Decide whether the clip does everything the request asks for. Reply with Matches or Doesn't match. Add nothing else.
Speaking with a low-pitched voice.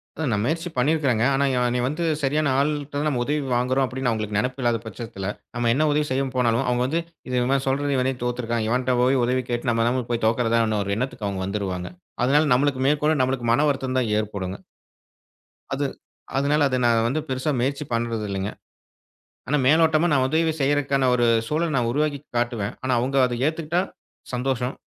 Matches